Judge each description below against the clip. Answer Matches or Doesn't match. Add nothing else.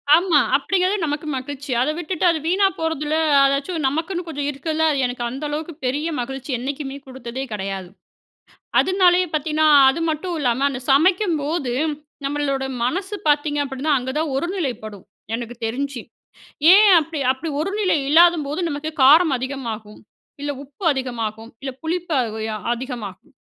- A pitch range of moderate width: Matches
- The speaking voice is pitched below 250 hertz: Doesn't match